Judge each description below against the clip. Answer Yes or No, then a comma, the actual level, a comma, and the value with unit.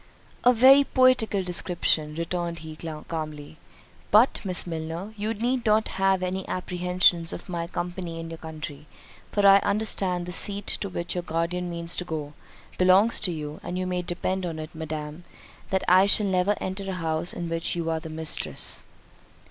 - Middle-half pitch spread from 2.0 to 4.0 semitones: Yes, average, 2.8 semitones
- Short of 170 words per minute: No, average, 180 wpm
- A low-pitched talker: No, medium, 180 Hz